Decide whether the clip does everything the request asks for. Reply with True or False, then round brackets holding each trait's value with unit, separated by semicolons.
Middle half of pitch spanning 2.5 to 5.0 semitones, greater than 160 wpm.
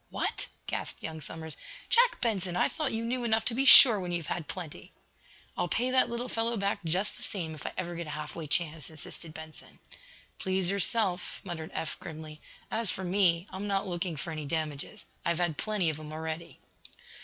True (4.7 semitones; 200 wpm)